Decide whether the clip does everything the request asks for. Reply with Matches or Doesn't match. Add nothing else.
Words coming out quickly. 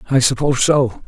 Doesn't match